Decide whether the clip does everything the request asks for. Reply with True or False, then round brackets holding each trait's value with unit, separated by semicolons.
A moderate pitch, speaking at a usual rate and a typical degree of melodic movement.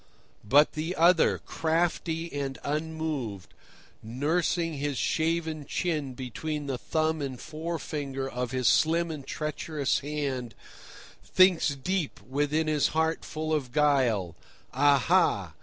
False (150 Hz; 115 wpm; 3.0 semitones)